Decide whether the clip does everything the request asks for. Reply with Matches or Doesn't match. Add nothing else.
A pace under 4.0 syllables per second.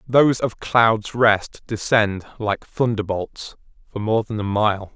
Matches